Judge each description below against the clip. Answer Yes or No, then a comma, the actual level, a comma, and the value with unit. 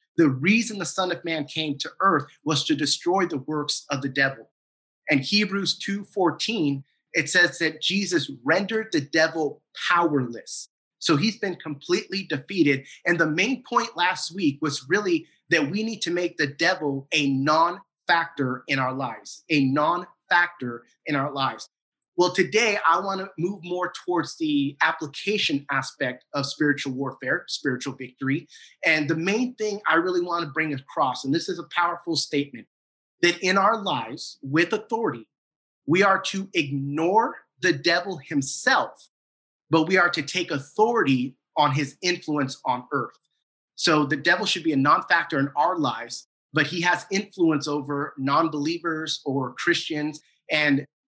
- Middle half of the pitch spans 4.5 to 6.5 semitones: No, average, 4.1 semitones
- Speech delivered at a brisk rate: No, average, 155 wpm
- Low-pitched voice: No, medium, 160 Hz